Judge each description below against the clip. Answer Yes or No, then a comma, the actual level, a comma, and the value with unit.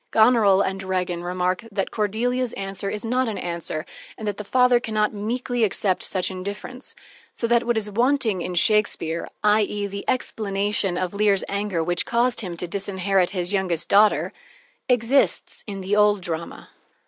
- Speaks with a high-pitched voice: Yes, high, 205 Hz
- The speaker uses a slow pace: No, average, 165 wpm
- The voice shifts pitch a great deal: No, average, 3.0 semitones